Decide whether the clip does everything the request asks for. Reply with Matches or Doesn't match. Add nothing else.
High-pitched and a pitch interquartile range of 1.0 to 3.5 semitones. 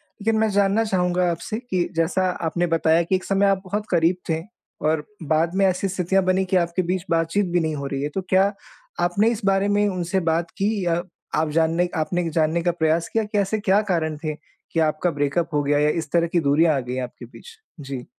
Doesn't match